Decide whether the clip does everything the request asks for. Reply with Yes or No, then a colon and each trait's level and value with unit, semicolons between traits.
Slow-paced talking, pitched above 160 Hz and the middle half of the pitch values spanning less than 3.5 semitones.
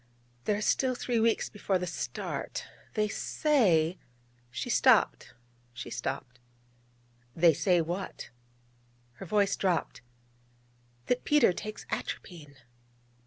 No: slow, 110 wpm; medium, 185 Hz; average, 4.8 semitones